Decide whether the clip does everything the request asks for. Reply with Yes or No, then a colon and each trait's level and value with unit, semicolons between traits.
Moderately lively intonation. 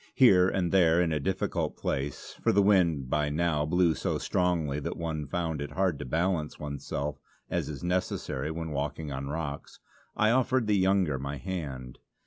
Yes: average, 4.0 semitones